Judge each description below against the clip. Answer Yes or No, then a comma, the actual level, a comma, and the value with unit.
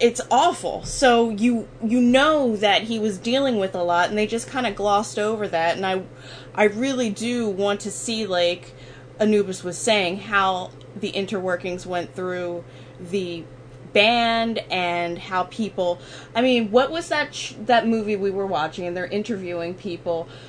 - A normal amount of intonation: Yes, average, 4.5 semitones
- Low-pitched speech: No, high, 200 Hz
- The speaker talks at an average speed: Yes, average, 170 wpm